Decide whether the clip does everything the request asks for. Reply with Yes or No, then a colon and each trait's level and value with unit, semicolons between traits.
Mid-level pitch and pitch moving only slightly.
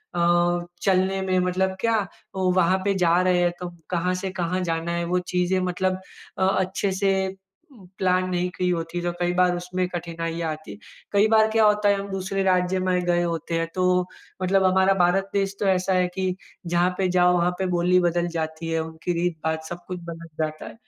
Yes: medium, 180 Hz; narrow, 1.5 semitones